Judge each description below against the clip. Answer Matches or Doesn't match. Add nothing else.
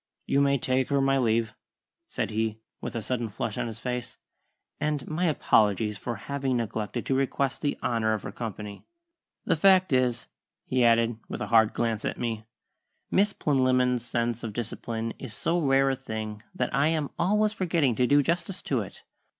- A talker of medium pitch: Doesn't match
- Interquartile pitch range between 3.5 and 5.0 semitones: Matches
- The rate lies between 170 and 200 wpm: Matches